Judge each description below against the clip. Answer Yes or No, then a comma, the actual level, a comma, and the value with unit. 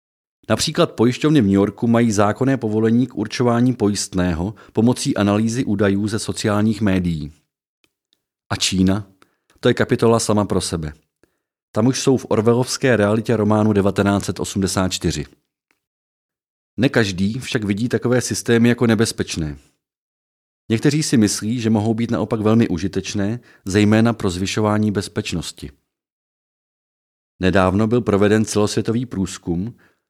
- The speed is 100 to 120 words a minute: Yes, slow, 115 wpm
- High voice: No, low, 105 Hz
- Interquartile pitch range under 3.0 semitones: No, average, 3.4 semitones